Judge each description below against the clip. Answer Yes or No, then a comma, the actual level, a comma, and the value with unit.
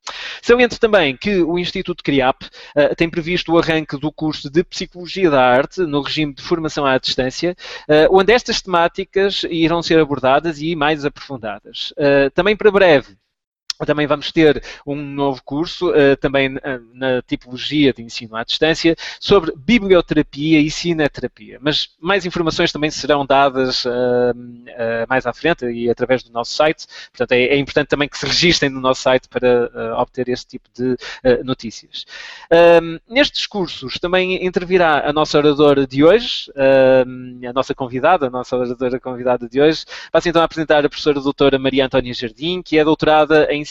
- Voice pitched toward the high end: No, medium, 145 Hz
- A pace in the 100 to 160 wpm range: No, average, 170 wpm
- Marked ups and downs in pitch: No, average, 4.4 semitones